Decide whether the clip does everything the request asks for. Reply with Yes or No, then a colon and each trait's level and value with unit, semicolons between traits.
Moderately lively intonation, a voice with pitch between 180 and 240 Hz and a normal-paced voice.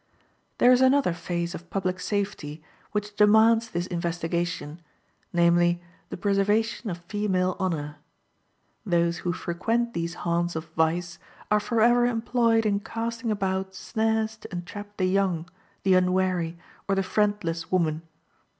No: average, 3.9 semitones; high, 190 Hz; slow, 130 wpm